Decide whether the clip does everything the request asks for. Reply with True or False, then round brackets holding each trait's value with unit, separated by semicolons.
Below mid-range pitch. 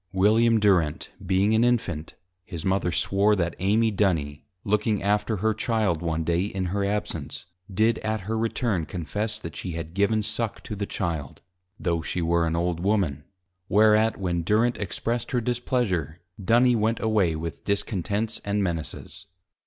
True (100 Hz)